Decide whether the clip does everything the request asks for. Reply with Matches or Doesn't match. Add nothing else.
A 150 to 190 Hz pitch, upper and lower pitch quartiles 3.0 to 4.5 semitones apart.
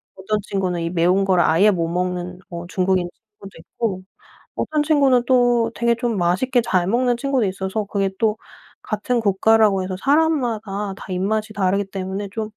Doesn't match